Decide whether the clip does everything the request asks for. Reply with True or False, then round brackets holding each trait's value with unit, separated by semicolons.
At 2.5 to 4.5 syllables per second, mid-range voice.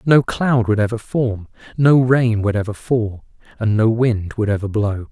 False (4.3 syllables/s; 115 Hz)